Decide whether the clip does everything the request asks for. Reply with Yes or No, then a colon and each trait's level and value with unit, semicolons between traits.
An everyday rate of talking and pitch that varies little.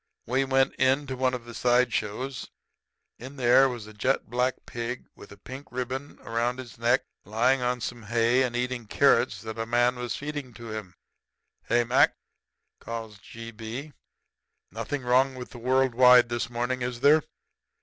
Yes: average, 170 wpm; narrow, 2.0 semitones